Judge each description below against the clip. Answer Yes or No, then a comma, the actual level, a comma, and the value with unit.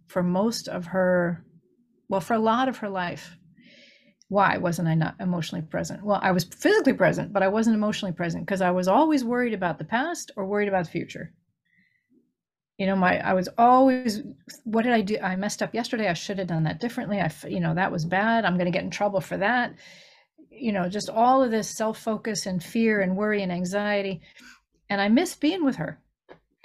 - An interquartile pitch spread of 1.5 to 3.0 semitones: No, average, 4.0 semitones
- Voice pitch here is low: No, high, 200 Hz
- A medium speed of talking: No, fast, 210 wpm